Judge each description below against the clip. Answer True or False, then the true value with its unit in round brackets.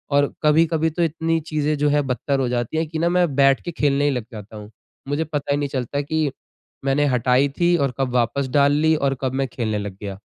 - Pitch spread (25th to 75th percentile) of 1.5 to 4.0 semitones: True (3.3 semitones)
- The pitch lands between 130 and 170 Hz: True (140 Hz)